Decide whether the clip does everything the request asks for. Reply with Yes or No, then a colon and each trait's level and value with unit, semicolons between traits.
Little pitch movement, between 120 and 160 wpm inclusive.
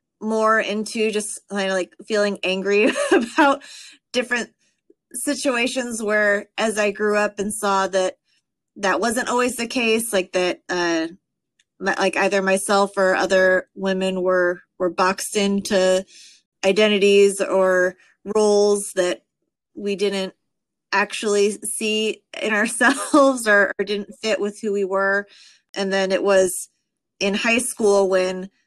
Yes: narrow, 2.3 semitones; slow, 135 wpm